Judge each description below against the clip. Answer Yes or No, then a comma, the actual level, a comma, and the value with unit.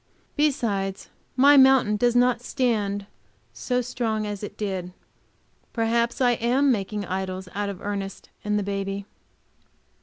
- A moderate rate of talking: No, slow, 130 wpm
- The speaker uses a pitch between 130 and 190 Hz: No, high, 210 Hz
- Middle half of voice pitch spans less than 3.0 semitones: No, average, 3.7 semitones